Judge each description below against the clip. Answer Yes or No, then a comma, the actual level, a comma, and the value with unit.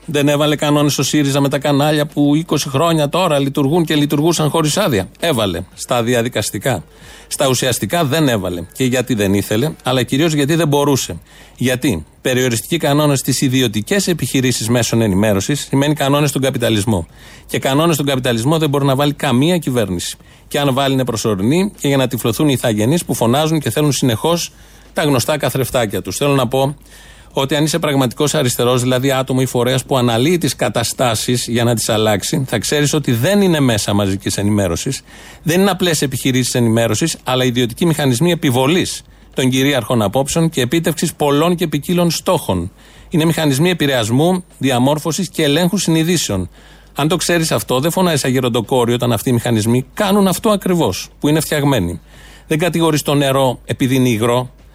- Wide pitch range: No, average, 4.0 semitones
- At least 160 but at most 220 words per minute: Yes, average, 165 wpm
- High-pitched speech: No, medium, 140 Hz